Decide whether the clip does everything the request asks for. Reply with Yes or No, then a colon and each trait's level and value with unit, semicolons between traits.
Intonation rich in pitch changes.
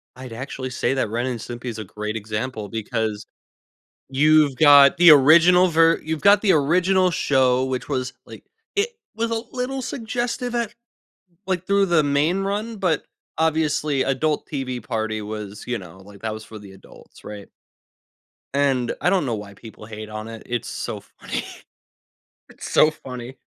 Yes: wide, 7.2 semitones